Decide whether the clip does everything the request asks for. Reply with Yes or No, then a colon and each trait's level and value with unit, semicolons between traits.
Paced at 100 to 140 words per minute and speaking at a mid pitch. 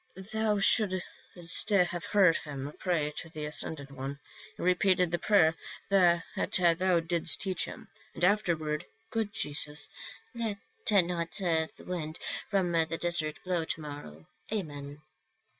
Yes: slow, 135 wpm; medium, 170 Hz